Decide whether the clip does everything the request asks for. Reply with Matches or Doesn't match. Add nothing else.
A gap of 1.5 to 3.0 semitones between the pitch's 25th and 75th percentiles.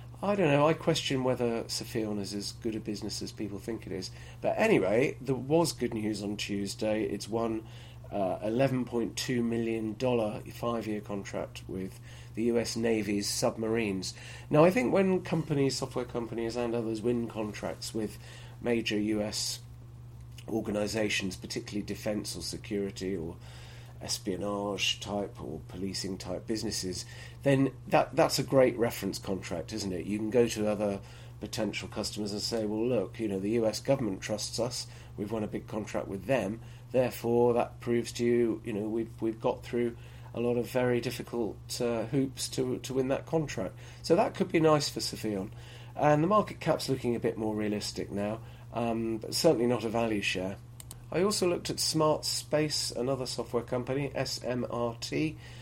Matches